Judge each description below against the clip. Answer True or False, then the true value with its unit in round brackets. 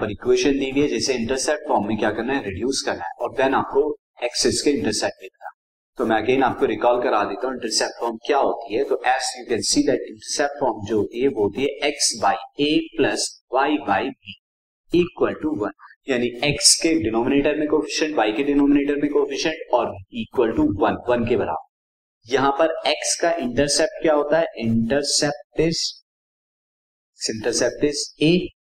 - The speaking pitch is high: False (145 Hz)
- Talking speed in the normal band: False (65 wpm)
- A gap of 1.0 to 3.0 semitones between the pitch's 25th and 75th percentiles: False (4.5 semitones)